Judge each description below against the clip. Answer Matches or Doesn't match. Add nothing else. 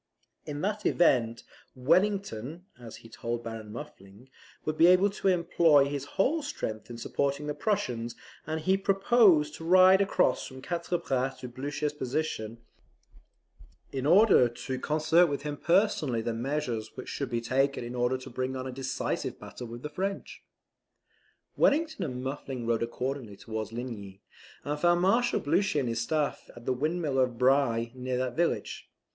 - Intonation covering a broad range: Matches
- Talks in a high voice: Doesn't match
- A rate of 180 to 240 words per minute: Doesn't match